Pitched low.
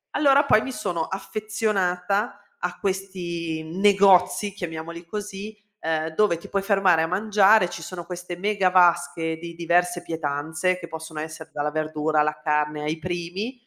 No: medium, 175 Hz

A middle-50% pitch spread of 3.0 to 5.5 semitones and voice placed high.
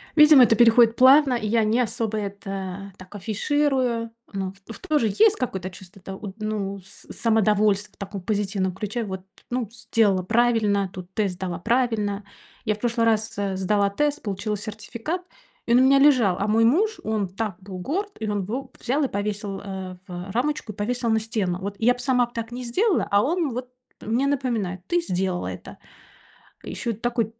Yes: average, 3.7 semitones; high, 220 Hz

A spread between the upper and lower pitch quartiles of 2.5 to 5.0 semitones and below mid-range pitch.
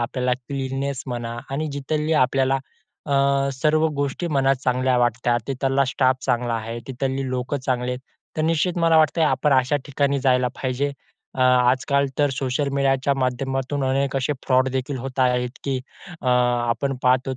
No: narrow, 1.7 semitones; low, 130 Hz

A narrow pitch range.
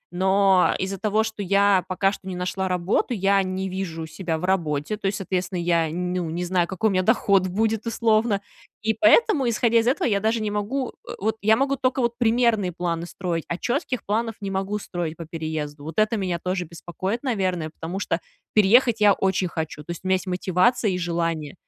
No: average, 3.8 semitones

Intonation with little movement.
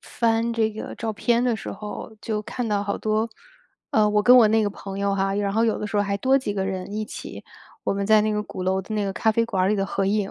Yes: narrow, 1.9 semitones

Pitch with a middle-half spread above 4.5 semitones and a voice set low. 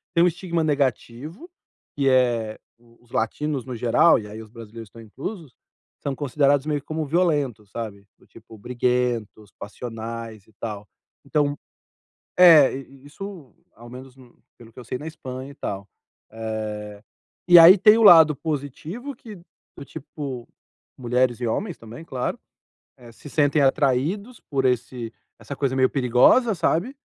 Yes: average, 5.0 semitones; low, 130 Hz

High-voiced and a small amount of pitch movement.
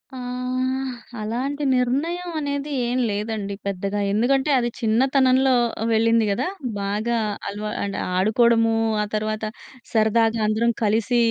No: high, 235 Hz; average, 3.2 semitones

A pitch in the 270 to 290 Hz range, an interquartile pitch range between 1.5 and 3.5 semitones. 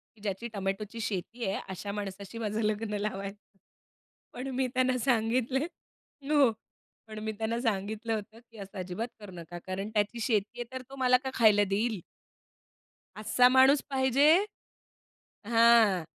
No: high, 220 Hz; average, 3.2 semitones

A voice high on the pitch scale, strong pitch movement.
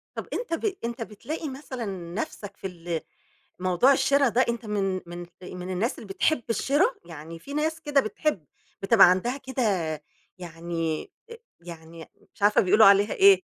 Yes: high, 210 Hz; wide, 7.3 semitones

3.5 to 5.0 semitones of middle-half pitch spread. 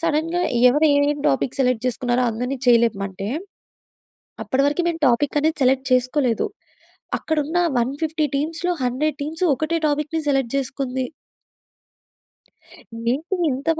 Yes: average, 3.8 semitones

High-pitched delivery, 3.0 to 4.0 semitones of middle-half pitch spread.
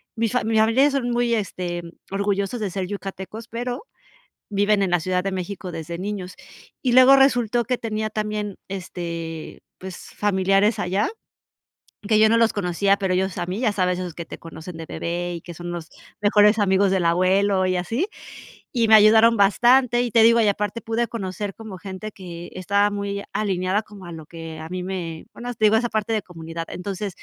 Yes: high, 200 Hz; average, 3.4 semitones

